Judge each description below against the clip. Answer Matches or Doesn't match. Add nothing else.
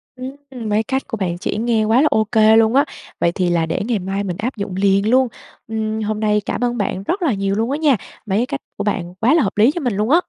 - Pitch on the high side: Matches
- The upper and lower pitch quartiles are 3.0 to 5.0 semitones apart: Matches